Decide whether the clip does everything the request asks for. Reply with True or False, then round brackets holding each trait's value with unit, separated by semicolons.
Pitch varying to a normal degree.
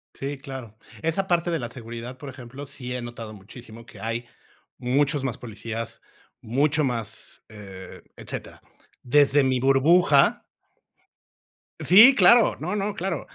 True (4.0 semitones)